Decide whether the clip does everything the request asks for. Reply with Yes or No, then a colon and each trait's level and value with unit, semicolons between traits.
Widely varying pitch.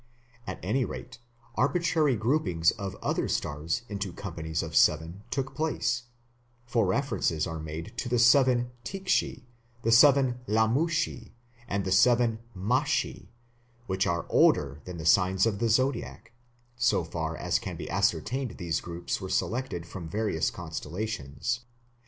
Yes: wide, 6.5 semitones